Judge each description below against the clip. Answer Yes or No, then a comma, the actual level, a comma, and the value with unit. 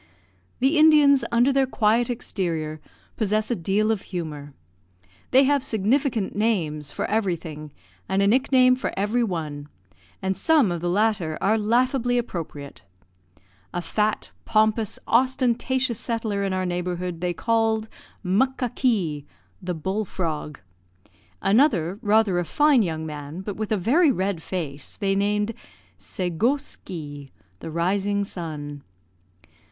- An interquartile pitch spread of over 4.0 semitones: Yes, wide, 5.6 semitones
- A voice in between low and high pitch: No, high, 200 Hz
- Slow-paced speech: Yes, slow, 125 wpm